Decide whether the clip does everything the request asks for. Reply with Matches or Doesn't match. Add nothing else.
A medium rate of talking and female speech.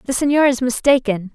Matches